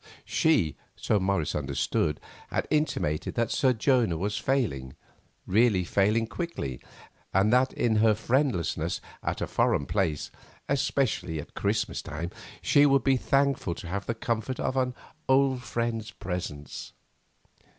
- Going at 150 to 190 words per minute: No, slow, 135 wpm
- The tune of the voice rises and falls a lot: Yes, wide, 7.1 semitones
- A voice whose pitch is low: Yes, low, 110 Hz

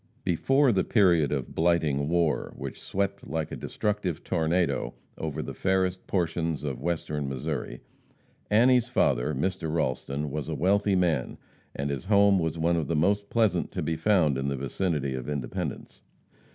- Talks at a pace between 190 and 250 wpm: No, average, 160 wpm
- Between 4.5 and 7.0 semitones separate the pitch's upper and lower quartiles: Yes, average, 4.9 semitones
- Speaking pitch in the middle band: No, very low, 85 Hz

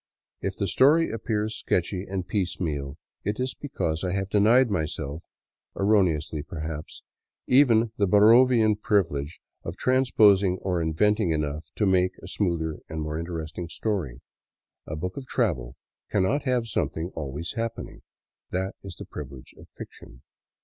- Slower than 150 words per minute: Yes, average, 140 wpm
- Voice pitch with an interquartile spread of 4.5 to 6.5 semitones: Yes, wide, 5.4 semitones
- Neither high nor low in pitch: No, very low, 95 Hz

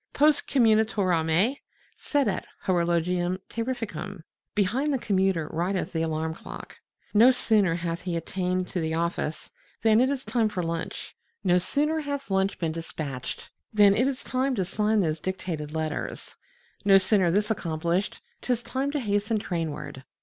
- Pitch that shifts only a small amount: No, average, 5.1 semitones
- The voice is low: No, high, 190 Hz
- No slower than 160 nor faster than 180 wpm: No, average, 150 wpm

